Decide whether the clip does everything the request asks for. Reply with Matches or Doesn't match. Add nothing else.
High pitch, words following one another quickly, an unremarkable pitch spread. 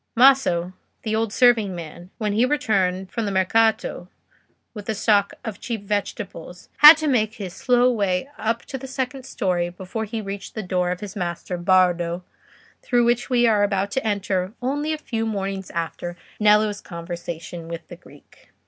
Doesn't match